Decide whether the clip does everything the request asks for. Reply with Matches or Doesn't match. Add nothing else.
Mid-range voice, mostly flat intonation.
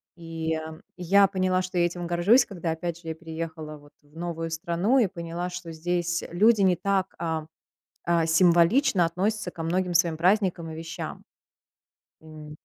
Matches